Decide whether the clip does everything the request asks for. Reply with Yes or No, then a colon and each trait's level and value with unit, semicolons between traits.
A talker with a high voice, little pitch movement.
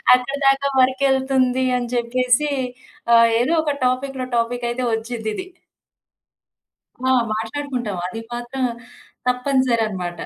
Yes: very high, 250 Hz; narrow, 2.2 semitones